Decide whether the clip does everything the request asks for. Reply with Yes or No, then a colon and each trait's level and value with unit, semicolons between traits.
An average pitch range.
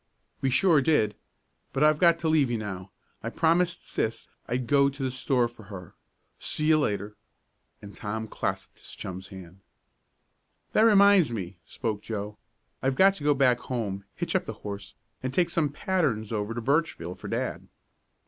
No: wide, 6.7 semitones